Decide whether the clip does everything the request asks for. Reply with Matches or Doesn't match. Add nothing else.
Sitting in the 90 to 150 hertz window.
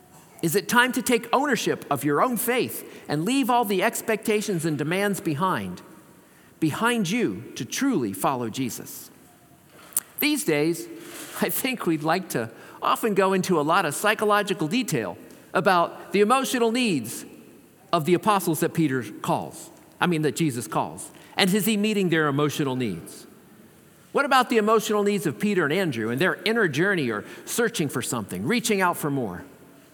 Doesn't match